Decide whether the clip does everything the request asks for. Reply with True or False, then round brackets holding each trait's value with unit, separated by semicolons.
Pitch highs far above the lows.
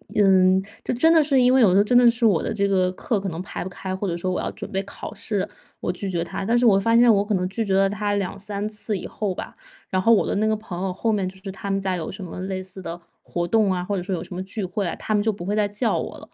False (2.4 semitones)